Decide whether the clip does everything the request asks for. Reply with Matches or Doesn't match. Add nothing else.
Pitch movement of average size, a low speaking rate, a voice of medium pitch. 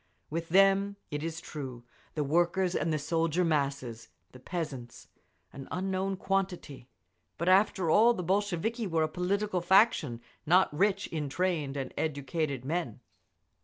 Matches